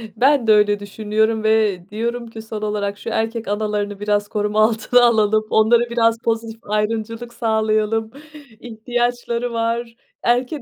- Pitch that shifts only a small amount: Yes, narrow, 1.7 semitones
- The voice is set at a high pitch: Yes, high, 220 Hz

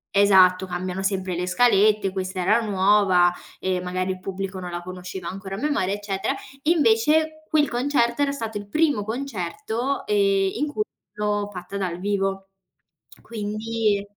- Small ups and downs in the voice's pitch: No, average, 3.6 semitones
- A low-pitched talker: No, high, 200 Hz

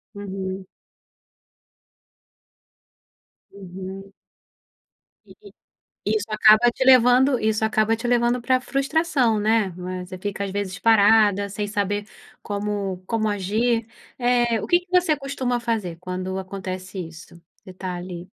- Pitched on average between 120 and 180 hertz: No, high, 210 Hz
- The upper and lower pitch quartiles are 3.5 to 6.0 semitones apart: Yes, average, 4.0 semitones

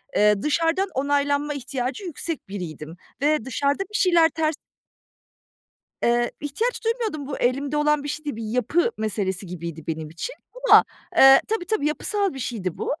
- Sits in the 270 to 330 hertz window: Yes, very high, 285 Hz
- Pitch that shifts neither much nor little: No, wide, 6.5 semitones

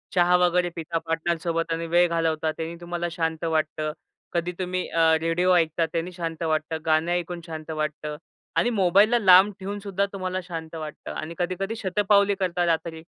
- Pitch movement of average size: No, narrow, 2.1 semitones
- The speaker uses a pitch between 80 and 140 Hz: No, medium, 170 Hz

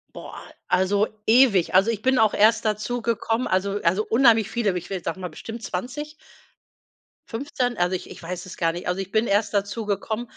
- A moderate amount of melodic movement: Yes, average, 3.6 semitones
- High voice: Yes, high, 210 Hz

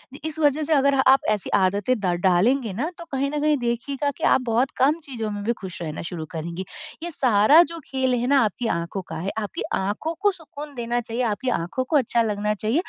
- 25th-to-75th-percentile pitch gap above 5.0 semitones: Yes, wide, 5.5 semitones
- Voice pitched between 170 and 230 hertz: No, high, 240 Hz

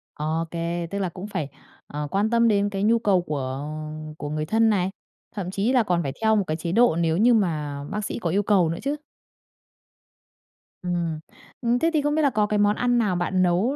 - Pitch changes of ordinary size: Yes, average, 4.8 semitones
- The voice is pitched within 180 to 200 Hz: Yes, high, 195 Hz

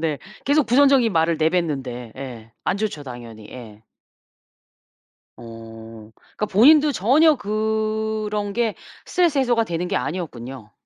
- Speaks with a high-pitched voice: No, medium, 180 Hz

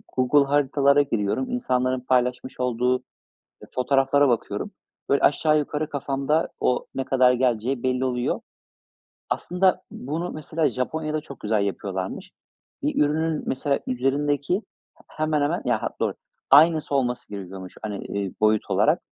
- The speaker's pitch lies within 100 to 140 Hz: Yes, low, 135 Hz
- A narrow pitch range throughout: No, average, 3.0 semitones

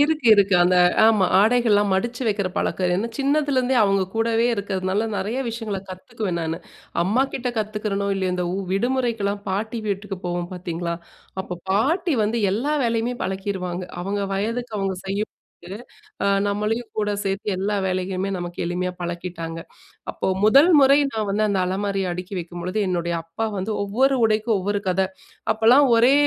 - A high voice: Yes, high, 200 Hz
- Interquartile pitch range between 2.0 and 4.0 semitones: Yes, average, 3.5 semitones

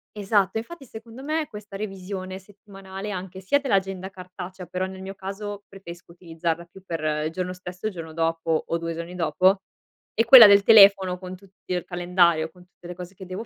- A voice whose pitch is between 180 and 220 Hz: Yes, high, 190 Hz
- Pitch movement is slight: Yes, narrow, 2.1 semitones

